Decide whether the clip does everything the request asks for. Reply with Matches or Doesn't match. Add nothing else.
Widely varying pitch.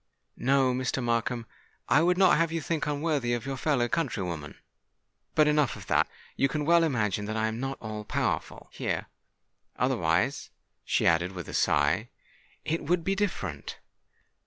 Matches